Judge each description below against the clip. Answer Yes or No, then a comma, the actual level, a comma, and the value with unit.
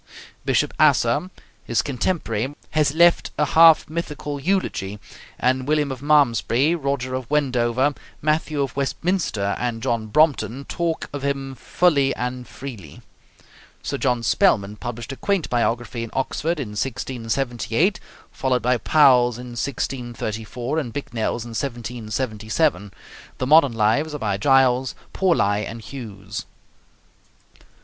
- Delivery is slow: Yes, slow, 125 wpm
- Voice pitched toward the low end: Yes, low, 130 Hz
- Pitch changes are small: No, average, 4.1 semitones